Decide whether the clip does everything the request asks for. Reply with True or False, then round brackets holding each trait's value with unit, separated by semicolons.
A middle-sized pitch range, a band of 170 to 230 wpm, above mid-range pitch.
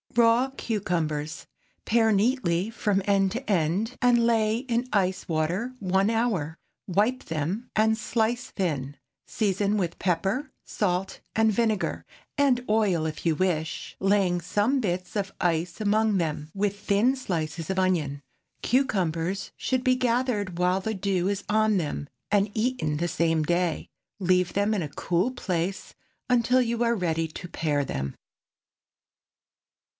False (4.7 semitones; 140 wpm; 195 Hz)